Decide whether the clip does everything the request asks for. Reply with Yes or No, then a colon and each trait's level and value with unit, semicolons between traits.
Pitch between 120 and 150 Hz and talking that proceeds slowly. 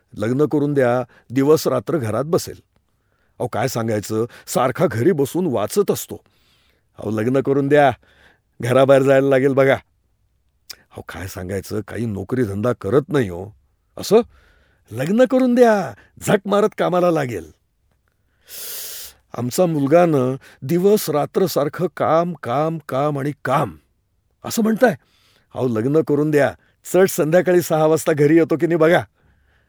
No: medium, 140 Hz; average, 135 wpm